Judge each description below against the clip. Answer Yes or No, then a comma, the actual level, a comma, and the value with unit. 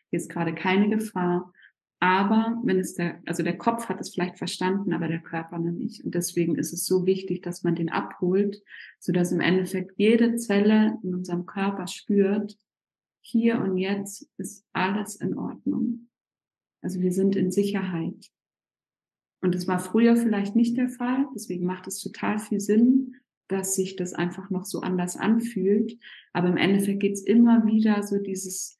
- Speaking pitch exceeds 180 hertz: Yes, high, 190 Hz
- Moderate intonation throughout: Yes, average, 3.1 semitones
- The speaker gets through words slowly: No, average, 175 wpm